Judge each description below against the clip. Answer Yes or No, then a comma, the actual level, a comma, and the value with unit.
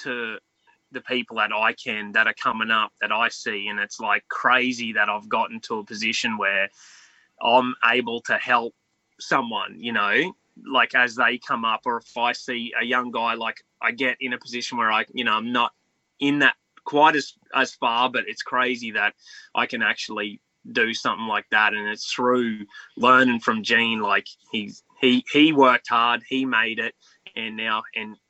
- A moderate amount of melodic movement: No, narrow, 1.8 semitones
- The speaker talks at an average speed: Yes, average, 190 wpm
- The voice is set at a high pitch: No, low, 120 Hz